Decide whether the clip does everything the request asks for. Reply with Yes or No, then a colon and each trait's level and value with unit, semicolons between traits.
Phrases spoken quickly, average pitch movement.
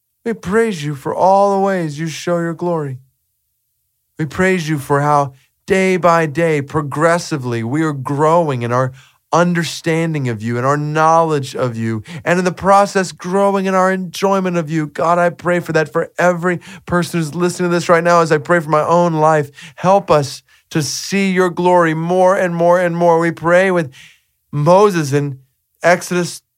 No: average, 185 wpm; average, 3.1 semitones